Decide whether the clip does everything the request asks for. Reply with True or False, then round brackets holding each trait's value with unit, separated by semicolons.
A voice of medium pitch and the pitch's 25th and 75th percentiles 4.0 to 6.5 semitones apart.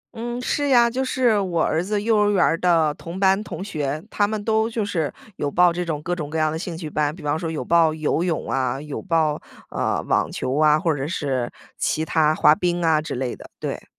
True (165 Hz; 4.6 semitones)